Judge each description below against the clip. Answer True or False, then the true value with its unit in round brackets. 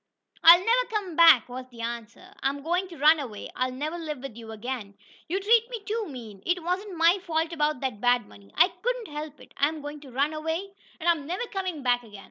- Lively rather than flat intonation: True (6.1 semitones)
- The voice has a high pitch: True (305 Hz)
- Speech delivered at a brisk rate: True (230 wpm)